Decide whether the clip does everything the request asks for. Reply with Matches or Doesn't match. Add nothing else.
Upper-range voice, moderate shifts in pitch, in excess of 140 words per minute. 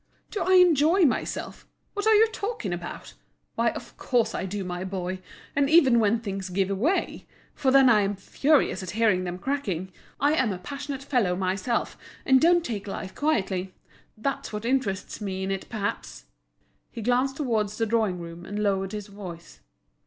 Doesn't match